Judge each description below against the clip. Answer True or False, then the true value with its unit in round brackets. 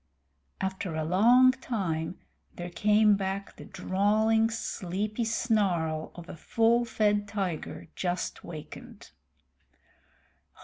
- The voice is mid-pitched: False (200 Hz)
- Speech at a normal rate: False (100 wpm)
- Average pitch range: True (3.9 semitones)